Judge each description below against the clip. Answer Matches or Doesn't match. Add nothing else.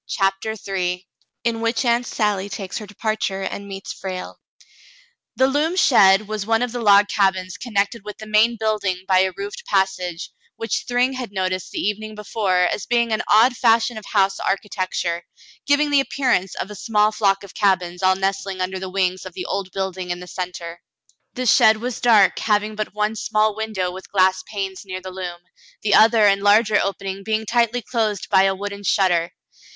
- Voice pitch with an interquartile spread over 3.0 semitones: Doesn't match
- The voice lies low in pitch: Doesn't match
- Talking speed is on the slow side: Doesn't match